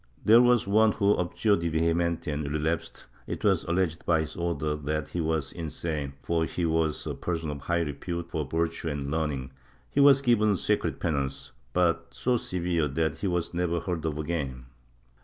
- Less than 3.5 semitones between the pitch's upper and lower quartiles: Yes, narrow, 2.5 semitones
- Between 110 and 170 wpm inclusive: No, average, 180 wpm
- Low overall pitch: Yes, very low, 85 Hz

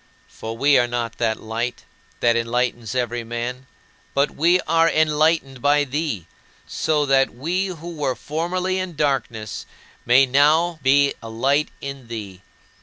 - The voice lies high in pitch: No, low, 135 Hz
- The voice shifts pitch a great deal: No, average, 4.6 semitones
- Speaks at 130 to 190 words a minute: Yes, average, 140 wpm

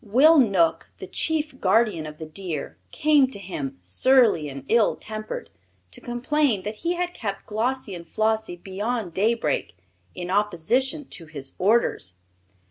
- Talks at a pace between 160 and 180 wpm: No, average, 145 wpm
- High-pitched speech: Yes, high, 210 Hz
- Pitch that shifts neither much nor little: No, wide, 6.5 semitones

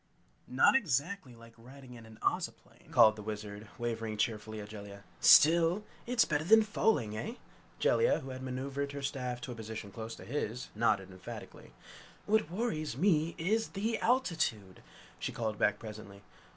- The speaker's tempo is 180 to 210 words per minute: No, average, 160 wpm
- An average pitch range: No, wide, 7.3 semitones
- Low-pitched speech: Yes, low, 125 Hz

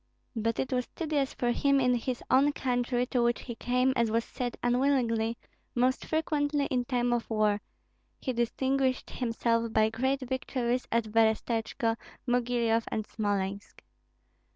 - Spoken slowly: No, average, 145 wpm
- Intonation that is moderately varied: No, narrow, 2.3 semitones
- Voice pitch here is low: No, high, 245 Hz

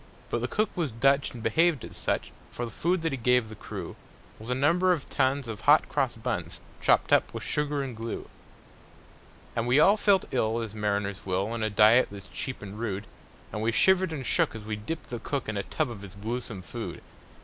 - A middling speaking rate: No, fast, 220 wpm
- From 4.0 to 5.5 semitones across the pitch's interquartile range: Yes, average, 5.1 semitones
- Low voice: Yes, low, 120 Hz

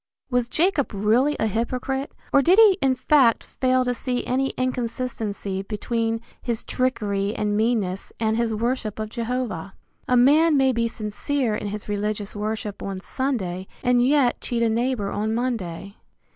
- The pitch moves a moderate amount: Yes, average, 3.4 semitones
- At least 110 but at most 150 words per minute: No, average, 160 wpm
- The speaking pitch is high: Yes, high, 235 Hz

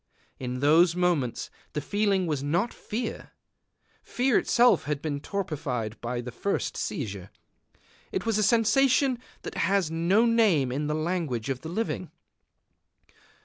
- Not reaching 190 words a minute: Yes, average, 140 wpm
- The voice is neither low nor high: Yes, medium, 165 Hz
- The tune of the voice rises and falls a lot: Yes, wide, 7.2 semitones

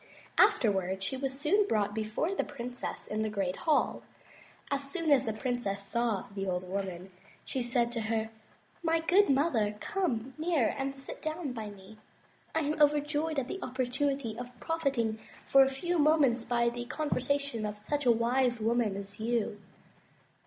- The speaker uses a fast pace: No, average, 165 wpm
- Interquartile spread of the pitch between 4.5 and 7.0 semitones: Yes, average, 4.9 semitones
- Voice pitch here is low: No, high, 245 Hz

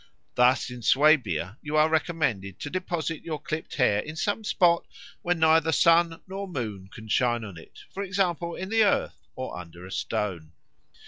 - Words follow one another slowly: No, average, 175 wpm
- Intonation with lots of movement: Yes, wide, 7.7 semitones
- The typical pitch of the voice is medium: Yes, medium, 155 Hz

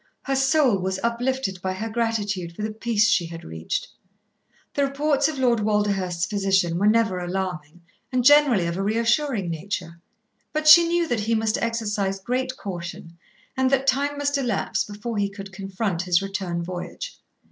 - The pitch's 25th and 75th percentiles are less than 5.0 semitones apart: No, wide, 5.4 semitones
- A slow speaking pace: No, average, 170 wpm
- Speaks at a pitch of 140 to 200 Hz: No, high, 210 Hz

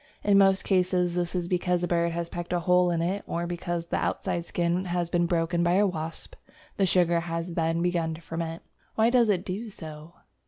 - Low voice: No, medium, 175 Hz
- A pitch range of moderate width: No, narrow, 1.2 semitones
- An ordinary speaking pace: No, fast, 210 wpm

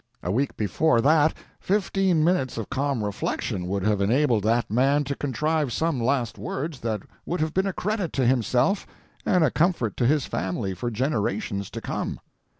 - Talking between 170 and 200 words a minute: Yes, average, 175 wpm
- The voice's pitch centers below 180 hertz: Yes, low, 135 Hz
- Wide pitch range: Yes, wide, 6.0 semitones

